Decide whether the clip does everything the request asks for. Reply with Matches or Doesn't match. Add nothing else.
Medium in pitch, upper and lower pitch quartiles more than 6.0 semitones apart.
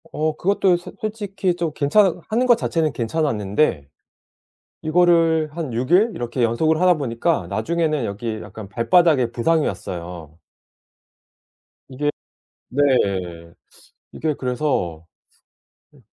Matches